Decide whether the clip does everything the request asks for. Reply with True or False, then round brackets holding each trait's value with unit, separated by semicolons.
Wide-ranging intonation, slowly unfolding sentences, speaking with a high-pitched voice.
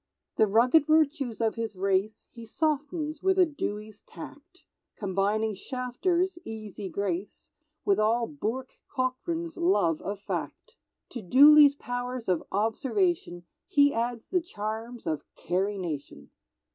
True (6.4 semitones; 125 wpm; 230 Hz)